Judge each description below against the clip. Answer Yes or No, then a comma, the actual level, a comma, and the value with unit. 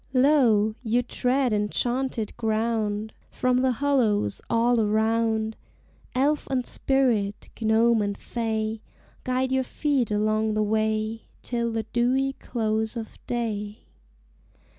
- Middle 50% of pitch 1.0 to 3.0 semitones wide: Yes, average, 2.7 semitones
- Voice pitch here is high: Yes, high, 225 Hz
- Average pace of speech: No, slow, 115 wpm